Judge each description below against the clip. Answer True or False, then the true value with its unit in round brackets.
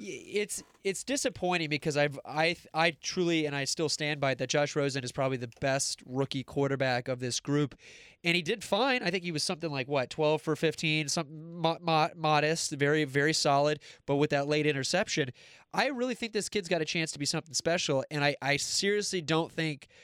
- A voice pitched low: False (155 Hz)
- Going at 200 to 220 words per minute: True (205 wpm)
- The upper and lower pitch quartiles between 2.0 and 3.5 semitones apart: True (3.2 semitones)